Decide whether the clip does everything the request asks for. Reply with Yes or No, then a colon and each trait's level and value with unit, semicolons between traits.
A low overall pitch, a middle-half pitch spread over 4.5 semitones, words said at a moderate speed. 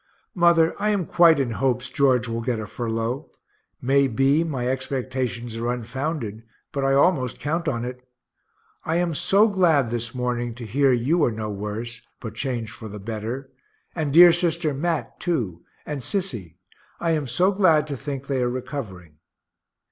Yes: low, 130 Hz; average, 5.2 semitones; average, 170 wpm